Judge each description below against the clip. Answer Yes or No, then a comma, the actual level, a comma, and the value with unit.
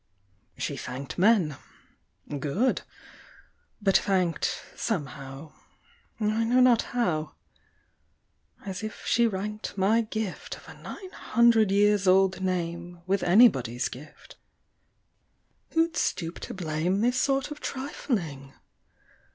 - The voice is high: Yes, high, 195 Hz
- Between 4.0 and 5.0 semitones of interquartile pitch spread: No, wide, 5.6 semitones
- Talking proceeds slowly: Yes, slow, 110 wpm